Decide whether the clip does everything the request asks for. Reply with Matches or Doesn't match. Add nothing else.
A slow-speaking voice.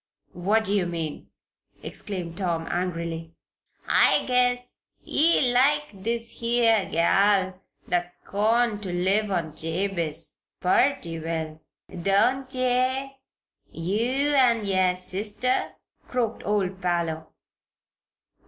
Matches